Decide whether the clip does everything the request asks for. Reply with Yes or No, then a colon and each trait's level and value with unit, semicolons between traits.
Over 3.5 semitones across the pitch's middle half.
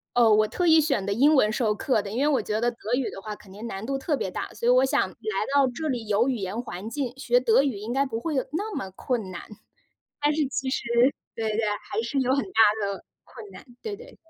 Yes: average, 4.5 semitones